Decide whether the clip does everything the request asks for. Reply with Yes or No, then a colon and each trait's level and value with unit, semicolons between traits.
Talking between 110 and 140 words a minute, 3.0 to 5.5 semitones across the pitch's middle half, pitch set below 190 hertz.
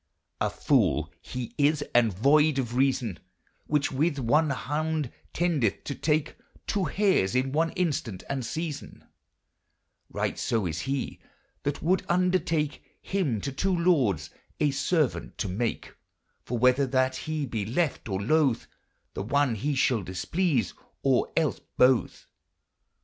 Yes: slow, 135 wpm; average, 4.7 semitones; medium, 140 Hz